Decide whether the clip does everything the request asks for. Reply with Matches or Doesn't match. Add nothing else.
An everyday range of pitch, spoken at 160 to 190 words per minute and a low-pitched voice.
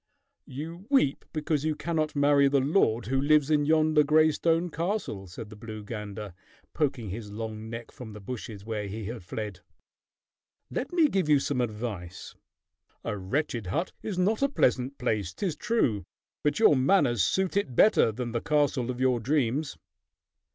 Doesn't match